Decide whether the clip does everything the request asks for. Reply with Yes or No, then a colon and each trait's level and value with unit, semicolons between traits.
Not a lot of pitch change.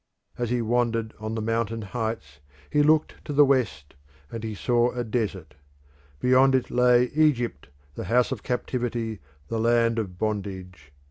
Yes: narrow, 2.3 semitones